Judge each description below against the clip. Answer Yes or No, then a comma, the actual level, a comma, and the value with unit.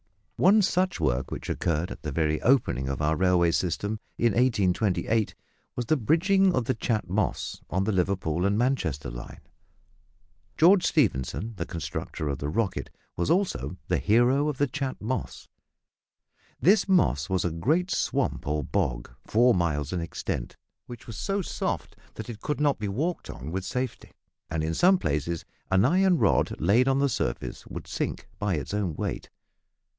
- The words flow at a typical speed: Yes, average, 170 wpm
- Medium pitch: No, low, 105 Hz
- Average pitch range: No, wide, 8.7 semitones